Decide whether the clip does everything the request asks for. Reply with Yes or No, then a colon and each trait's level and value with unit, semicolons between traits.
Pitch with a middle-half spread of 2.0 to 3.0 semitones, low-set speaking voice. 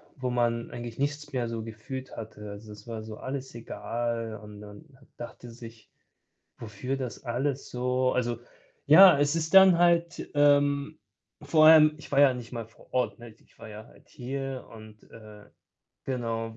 No: average, 3.9 semitones; low, 125 Hz